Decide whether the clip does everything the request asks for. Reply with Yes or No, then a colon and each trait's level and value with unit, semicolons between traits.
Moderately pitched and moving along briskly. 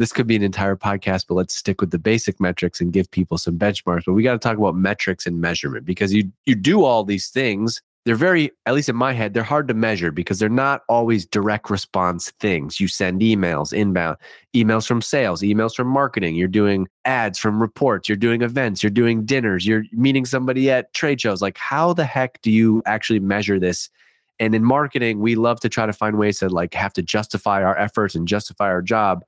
No: low, 105 Hz; fast, 225 wpm